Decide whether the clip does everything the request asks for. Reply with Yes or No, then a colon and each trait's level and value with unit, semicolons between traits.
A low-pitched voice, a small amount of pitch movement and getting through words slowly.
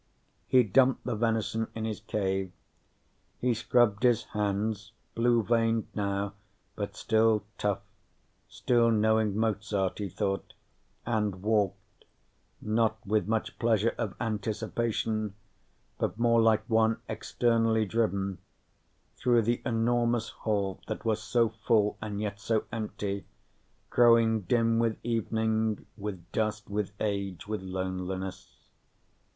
Yes: low, 110 Hz; narrow, 2.1 semitones; slow, 120 wpm